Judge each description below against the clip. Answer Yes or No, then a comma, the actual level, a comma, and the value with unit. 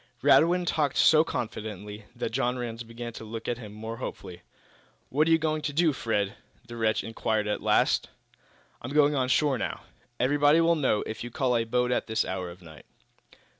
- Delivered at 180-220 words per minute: Yes, average, 200 wpm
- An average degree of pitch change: Yes, average, 4.9 semitones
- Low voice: Yes, low, 120 Hz